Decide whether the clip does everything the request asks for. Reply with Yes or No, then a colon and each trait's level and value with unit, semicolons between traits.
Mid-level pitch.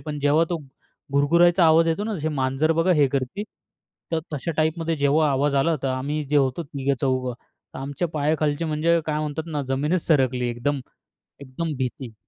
Yes: medium, 150 Hz